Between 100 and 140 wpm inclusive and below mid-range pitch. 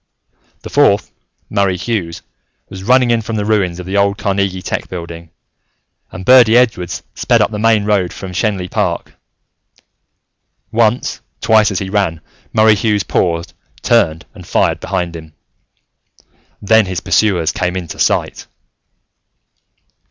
Yes: slow, 135 wpm; low, 100 Hz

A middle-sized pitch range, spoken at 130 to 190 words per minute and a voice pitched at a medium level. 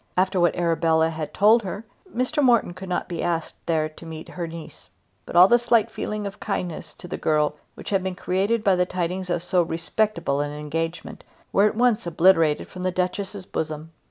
No: average, 3.4 semitones; average, 200 wpm; medium, 180 Hz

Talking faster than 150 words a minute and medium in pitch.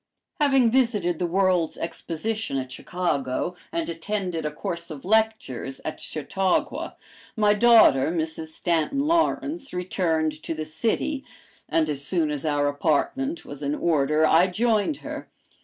No: average, 140 wpm; medium, 170 Hz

